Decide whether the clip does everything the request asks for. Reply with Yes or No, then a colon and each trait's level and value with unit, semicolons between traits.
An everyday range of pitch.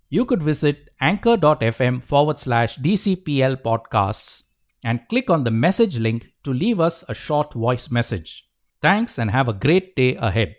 No: wide, 6.4 semitones